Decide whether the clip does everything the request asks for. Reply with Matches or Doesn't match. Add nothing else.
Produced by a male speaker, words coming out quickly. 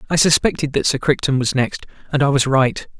Matches